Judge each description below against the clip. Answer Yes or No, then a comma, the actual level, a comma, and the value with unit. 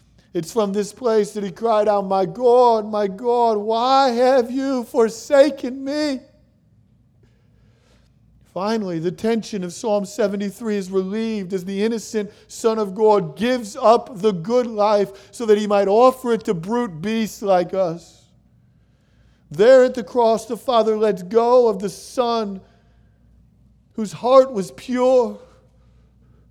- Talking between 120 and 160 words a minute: Yes, average, 140 wpm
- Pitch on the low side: No, high, 215 Hz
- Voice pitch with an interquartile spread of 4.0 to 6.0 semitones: No, average, 3.5 semitones